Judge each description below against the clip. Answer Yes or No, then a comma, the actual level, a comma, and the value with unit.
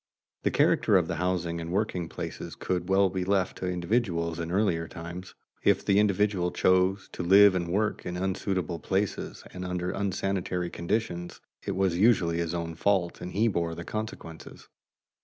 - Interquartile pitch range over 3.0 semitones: No, narrow, 2.4 semitones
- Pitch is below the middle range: Yes, very low, 90 Hz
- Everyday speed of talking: Yes, average, 170 wpm